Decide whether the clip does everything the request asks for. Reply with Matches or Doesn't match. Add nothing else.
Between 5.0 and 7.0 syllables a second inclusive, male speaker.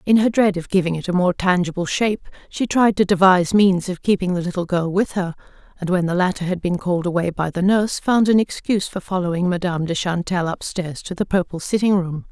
Doesn't match